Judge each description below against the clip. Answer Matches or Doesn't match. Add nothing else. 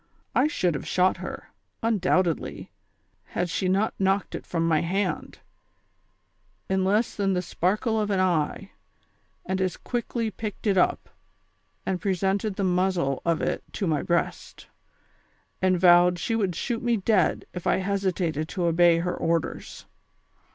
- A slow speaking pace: Doesn't match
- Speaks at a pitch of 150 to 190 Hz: Matches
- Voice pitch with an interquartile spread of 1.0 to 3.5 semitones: Matches